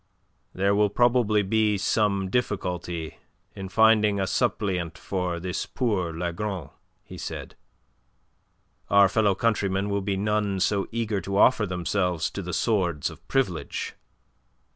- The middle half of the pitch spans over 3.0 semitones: No, average, 2.7 semitones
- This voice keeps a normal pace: No, slow, 130 wpm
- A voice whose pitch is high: No, low, 100 Hz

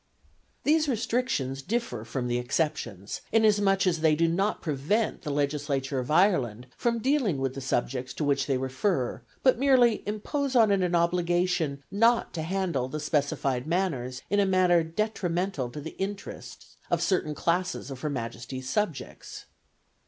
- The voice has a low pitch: No, medium, 165 Hz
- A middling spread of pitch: No, wide, 7.0 semitones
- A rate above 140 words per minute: Yes, average, 155 wpm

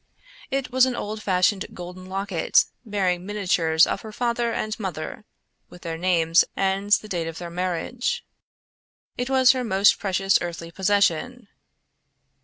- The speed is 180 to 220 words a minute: No, average, 145 wpm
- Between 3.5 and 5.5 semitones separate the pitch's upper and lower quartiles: Yes, average, 3.8 semitones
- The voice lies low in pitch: No, high, 195 Hz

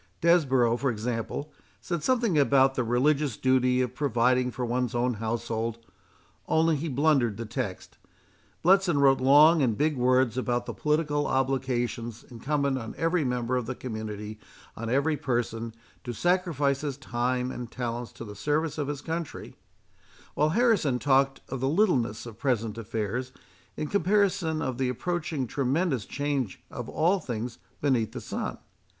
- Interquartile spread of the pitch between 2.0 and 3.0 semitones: No, average, 3.9 semitones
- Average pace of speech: Yes, average, 155 wpm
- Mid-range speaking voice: No, low, 130 Hz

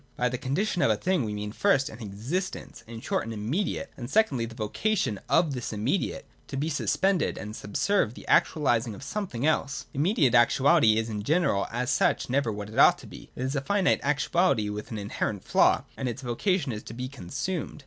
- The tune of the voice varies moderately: No, wide, 6.6 semitones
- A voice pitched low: Yes, low, 130 Hz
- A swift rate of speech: Yes, fast, 210 wpm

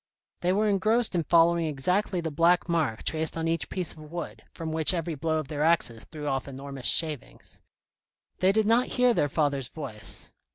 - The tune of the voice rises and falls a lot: No, average, 3.6 semitones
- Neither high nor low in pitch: Yes, medium, 165 Hz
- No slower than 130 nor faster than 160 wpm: No, average, 190 wpm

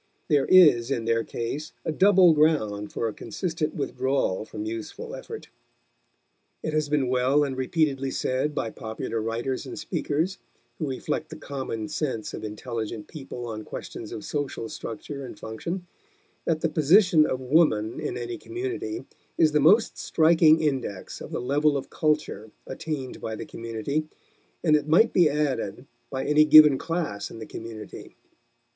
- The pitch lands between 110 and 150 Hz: Yes, medium, 140 Hz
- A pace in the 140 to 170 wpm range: Yes, average, 160 wpm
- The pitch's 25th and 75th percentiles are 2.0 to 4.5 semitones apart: No, average, 5.2 semitones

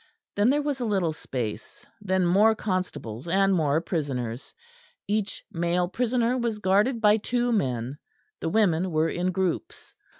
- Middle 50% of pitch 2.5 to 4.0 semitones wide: No, average, 5.3 semitones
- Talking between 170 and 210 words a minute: No, average, 155 wpm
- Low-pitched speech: No, high, 190 Hz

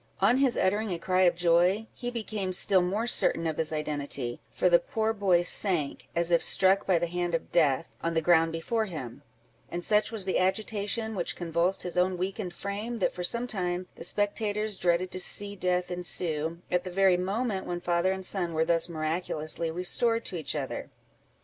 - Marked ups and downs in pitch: No, average, 3.0 semitones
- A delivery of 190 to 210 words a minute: Yes, average, 195 wpm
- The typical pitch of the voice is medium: Yes, medium, 180 Hz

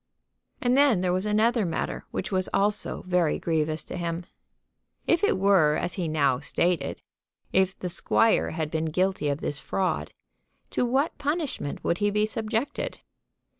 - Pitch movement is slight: No, average, 5.0 semitones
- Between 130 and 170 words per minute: Yes, average, 160 wpm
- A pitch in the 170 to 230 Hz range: Yes, medium, 185 Hz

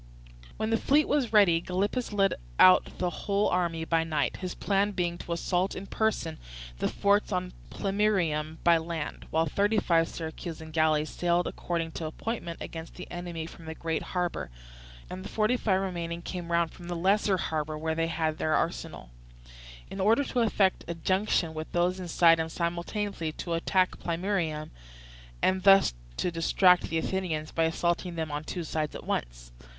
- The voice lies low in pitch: No, medium, 175 Hz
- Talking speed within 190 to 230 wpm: No, average, 175 wpm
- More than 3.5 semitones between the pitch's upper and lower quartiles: No, average, 2.9 semitones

